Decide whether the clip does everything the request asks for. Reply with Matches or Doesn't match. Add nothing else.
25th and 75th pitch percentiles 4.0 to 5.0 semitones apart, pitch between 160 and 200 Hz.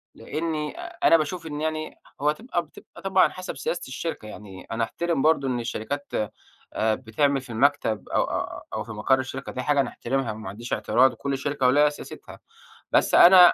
Doesn't match